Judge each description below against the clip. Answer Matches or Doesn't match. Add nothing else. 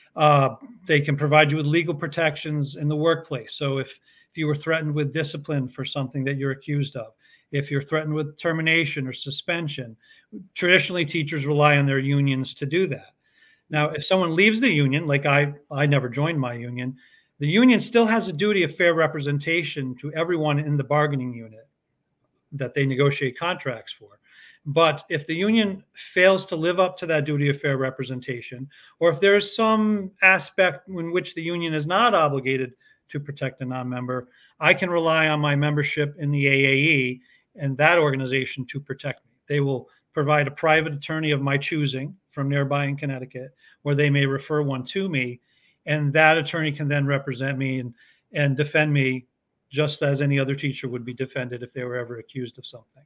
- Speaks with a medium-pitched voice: Matches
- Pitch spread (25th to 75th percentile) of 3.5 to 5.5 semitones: Doesn't match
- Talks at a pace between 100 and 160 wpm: Doesn't match